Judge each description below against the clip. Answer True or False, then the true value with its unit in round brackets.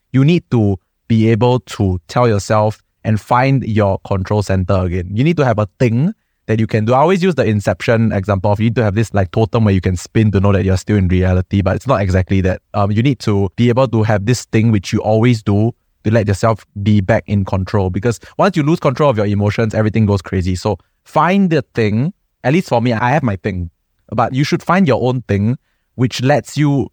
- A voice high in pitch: False (110 Hz)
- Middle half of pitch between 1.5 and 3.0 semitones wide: False (3.8 semitones)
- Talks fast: True (240 wpm)